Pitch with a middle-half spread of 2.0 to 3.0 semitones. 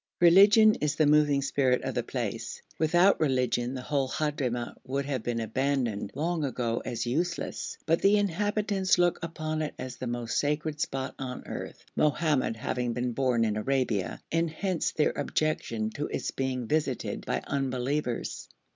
No: average, 4.0 semitones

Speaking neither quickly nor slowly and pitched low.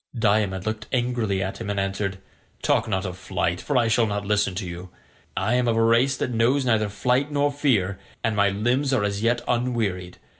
No: fast, 210 wpm; low, 110 Hz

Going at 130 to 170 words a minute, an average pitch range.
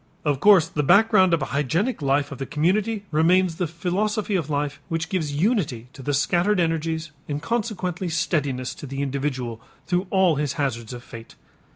No: average, 180 wpm; average, 4.9 semitones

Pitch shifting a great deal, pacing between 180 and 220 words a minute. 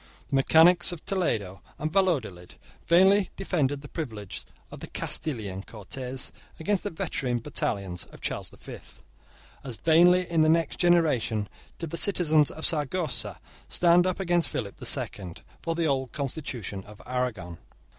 No: wide, 7.2 semitones; average, 150 wpm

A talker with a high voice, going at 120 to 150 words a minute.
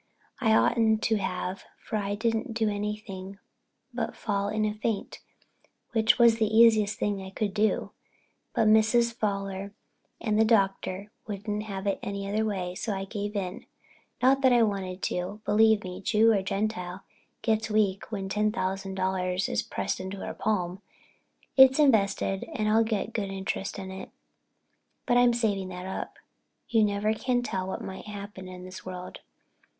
No: high, 205 Hz; average, 170 wpm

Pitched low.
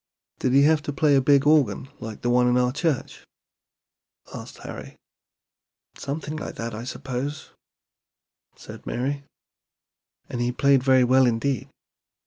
Yes: low, 130 Hz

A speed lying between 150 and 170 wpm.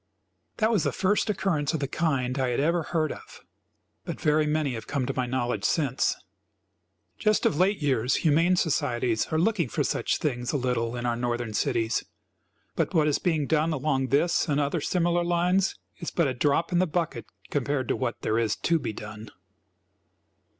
No: average, 190 wpm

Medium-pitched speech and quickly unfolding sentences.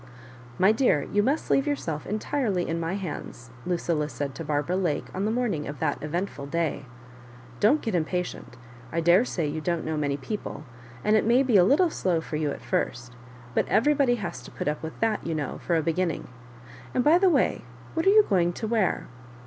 Yes: medium, 175 Hz; fast, 215 wpm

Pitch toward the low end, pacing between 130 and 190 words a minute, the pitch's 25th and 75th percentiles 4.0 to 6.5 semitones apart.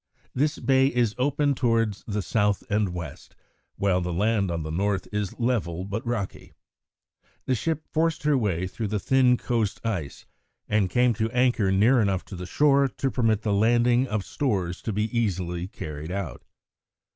Yes: low, 105 Hz; average, 170 wpm; average, 4.6 semitones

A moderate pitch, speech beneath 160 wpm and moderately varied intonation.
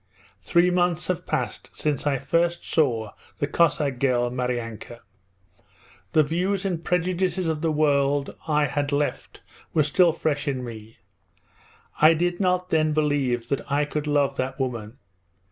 Yes: medium, 150 Hz; average, 145 wpm; average, 4.1 semitones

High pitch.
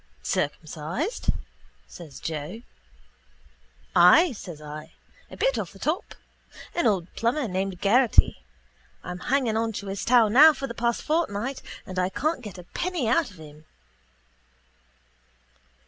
Yes: high, 210 Hz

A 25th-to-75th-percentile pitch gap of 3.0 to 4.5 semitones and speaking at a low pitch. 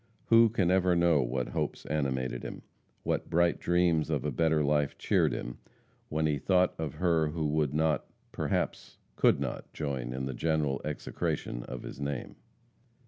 Yes: average, 3.7 semitones; very low, 75 Hz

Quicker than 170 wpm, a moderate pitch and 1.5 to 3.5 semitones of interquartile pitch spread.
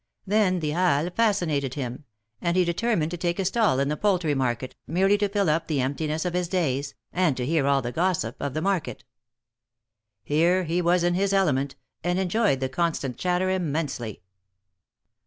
No: average, 180 wpm; medium, 170 Hz; average, 4.7 semitones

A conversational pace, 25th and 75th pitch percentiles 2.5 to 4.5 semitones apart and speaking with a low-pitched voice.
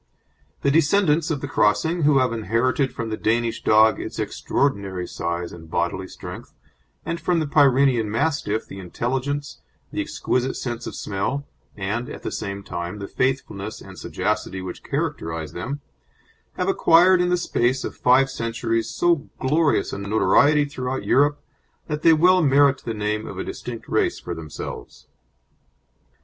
No: average, 155 wpm; wide, 5.6 semitones; low, 125 Hz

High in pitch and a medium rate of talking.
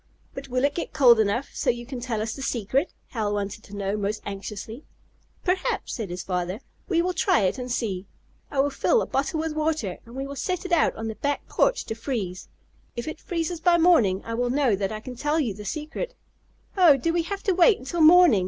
No: very high, 255 Hz; fast, 230 wpm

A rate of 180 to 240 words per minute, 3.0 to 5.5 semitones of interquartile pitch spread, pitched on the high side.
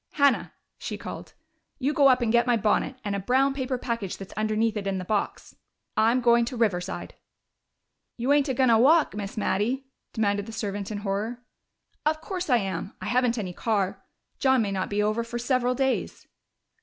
Yes: average, 195 wpm; average, 3.9 semitones; high, 230 Hz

